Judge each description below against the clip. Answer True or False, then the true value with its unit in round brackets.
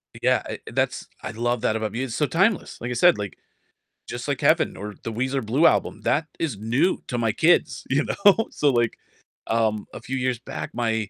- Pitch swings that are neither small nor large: True (4.4 semitones)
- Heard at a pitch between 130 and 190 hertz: False (120 Hz)